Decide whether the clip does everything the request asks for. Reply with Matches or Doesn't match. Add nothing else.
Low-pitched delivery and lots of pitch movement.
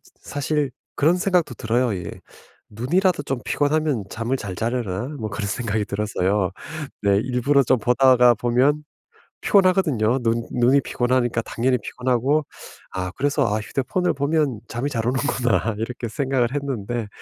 Doesn't match